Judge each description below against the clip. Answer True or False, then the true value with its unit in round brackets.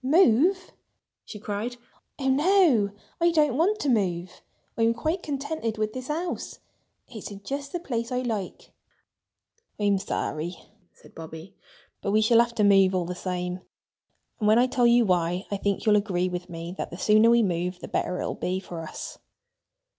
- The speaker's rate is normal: True (180 wpm)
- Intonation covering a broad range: True (5.8 semitones)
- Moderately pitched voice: False (215 Hz)